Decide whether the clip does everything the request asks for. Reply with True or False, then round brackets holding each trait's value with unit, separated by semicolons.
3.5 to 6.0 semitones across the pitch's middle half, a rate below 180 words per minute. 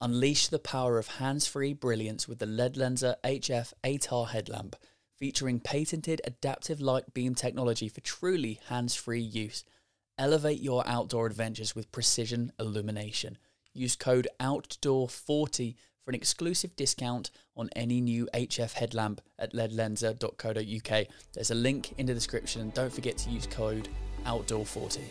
False (2.9 semitones; 135 wpm)